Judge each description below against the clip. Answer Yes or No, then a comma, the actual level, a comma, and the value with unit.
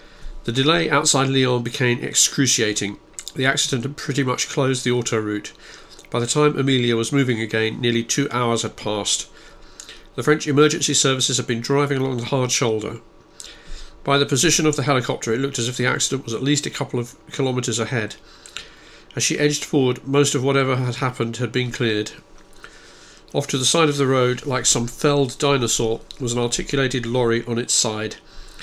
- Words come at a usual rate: Yes, average, 185 wpm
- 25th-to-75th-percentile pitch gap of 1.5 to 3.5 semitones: Yes, average, 3.0 semitones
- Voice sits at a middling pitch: No, low, 130 Hz